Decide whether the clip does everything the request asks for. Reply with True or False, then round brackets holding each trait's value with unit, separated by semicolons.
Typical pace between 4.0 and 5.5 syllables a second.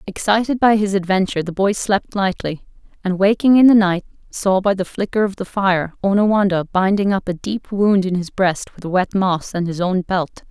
True (5.0 syllables/s)